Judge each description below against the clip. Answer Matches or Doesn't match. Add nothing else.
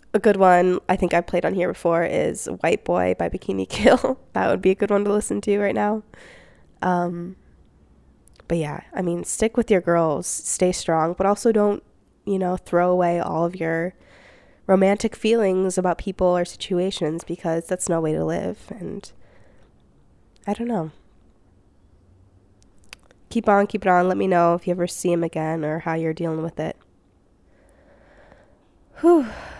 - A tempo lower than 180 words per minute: Matches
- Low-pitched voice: Doesn't match